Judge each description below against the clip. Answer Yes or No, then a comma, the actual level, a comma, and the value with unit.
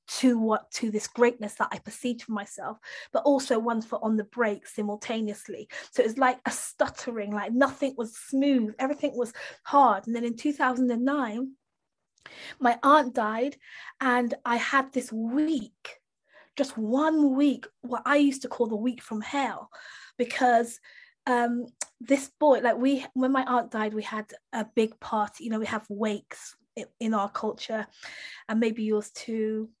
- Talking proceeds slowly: No, average, 165 wpm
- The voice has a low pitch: No, high, 240 Hz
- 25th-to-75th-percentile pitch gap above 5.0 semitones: No, average, 3.6 semitones